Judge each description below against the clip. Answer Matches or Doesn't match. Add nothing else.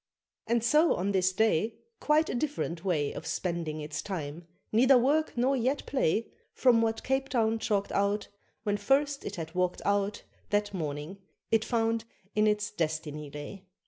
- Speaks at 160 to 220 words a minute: Matches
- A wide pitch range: Matches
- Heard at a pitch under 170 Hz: Doesn't match